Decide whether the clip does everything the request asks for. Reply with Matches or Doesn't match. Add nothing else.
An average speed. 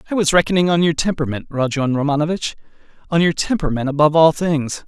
Matches